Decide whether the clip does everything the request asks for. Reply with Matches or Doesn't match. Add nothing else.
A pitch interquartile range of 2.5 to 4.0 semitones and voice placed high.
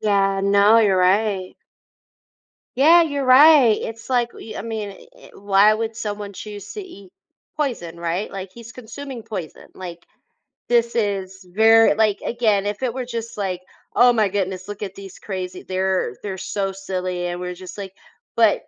Matches